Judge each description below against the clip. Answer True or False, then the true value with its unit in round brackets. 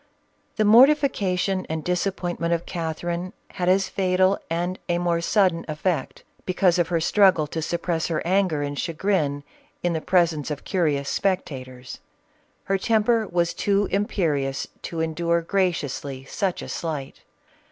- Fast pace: False (145 wpm)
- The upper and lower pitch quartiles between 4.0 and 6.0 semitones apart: False (3.1 semitones)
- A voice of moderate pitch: True (175 Hz)